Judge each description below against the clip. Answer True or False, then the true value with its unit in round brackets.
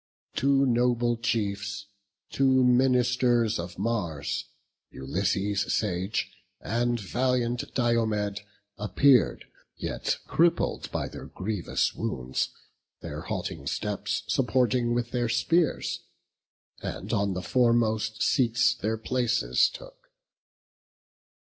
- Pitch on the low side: True (120 Hz)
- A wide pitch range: False (3.5 semitones)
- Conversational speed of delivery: False (95 wpm)